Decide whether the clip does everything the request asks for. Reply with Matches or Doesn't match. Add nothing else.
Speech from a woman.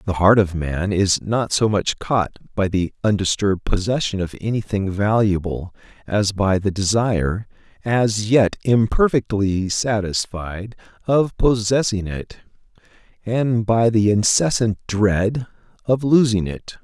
Doesn't match